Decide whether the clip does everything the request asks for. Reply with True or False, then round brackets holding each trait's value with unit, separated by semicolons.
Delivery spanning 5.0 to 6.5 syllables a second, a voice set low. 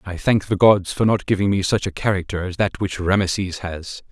True (5.4 syllables/s; 95 Hz)